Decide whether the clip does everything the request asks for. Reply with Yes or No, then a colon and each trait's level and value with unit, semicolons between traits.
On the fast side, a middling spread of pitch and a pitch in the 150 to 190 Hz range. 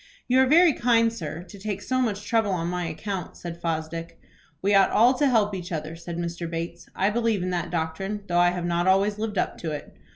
Yes: fast, 230 wpm; average, 3.9 semitones; medium, 185 Hz